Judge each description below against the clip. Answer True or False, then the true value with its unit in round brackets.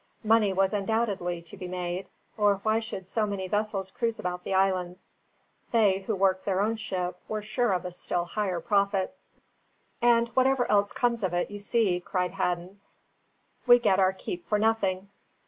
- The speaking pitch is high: True (195 Hz)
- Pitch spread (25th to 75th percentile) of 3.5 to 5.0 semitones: False (3.0 semitones)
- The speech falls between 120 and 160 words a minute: False (175 wpm)